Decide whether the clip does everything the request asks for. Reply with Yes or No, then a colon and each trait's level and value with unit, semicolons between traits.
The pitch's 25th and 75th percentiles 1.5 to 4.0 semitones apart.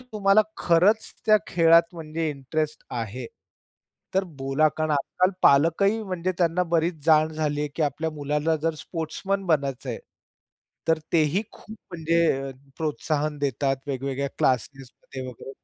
Yes: average, 3.2 semitones